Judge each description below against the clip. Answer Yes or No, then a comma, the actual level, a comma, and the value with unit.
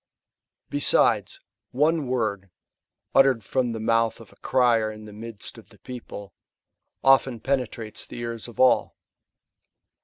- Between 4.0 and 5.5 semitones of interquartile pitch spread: No, average, 3.0 semitones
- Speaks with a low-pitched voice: Yes, low, 115 Hz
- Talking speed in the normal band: No, slow, 130 wpm